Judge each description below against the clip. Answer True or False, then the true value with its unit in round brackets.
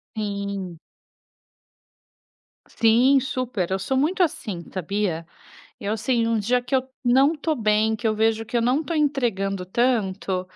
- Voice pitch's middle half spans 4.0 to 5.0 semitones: True (4.5 semitones)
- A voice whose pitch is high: True (225 Hz)